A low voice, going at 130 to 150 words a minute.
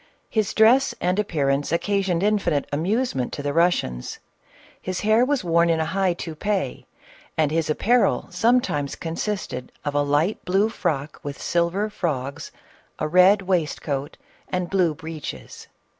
No: medium, 170 Hz; average, 140 wpm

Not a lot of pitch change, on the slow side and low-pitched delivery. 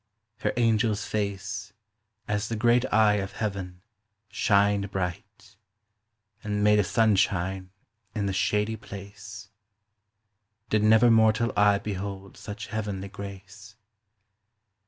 Yes: narrow, 1.6 semitones; slow, 110 wpm; low, 105 Hz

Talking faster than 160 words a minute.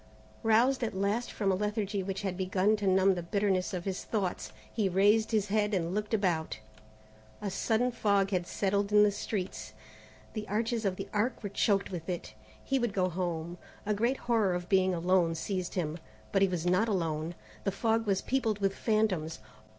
Yes: average, 190 wpm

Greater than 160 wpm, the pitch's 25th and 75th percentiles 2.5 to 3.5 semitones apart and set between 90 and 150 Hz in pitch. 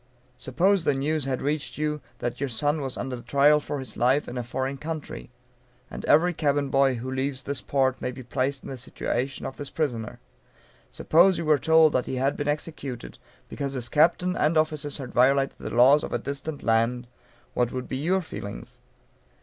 Yes: average, 195 wpm; average, 2.9 semitones; medium, 140 Hz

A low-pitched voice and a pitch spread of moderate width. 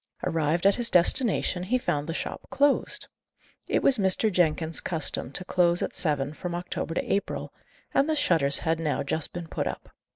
No: medium, 175 Hz; average, 4.0 semitones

